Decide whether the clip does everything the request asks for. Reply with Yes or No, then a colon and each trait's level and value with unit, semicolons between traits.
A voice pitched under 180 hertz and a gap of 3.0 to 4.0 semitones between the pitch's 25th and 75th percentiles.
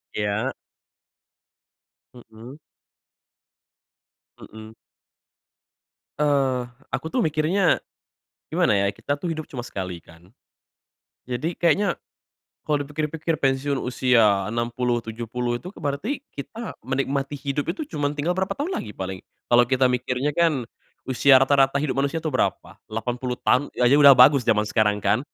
Yes: low, 135 Hz; average, 3.7 semitones